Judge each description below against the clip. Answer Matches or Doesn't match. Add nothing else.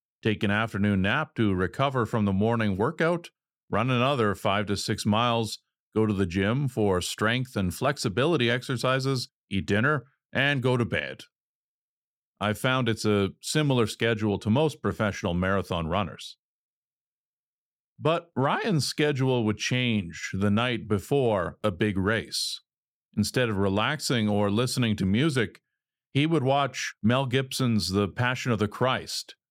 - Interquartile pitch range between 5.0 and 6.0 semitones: Doesn't match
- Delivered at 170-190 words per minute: Doesn't match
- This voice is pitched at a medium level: Doesn't match